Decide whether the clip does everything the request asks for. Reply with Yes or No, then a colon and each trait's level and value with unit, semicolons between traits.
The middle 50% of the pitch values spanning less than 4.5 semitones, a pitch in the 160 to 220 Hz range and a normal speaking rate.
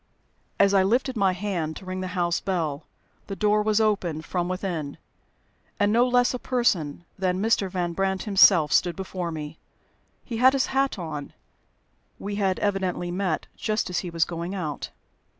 Yes: average, 3.3 semitones; high, 190 Hz; average, 170 wpm